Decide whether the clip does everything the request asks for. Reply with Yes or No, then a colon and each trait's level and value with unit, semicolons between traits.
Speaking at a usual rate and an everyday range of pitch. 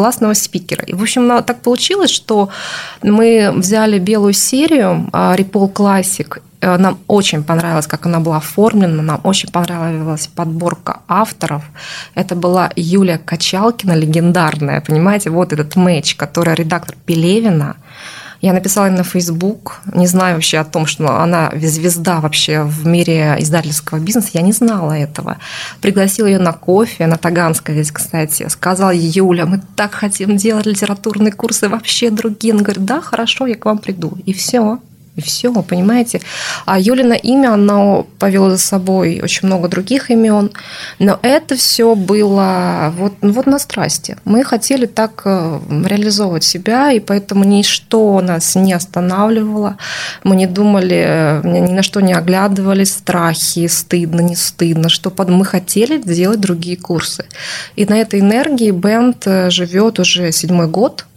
Yes: average, 145 wpm; average, 3.8 semitones